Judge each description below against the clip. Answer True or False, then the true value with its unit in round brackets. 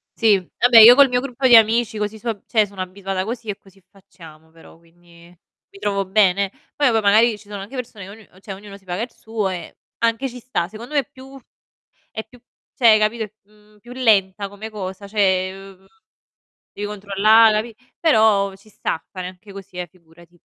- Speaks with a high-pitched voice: True (205 Hz)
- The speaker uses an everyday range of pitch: True (3.0 semitones)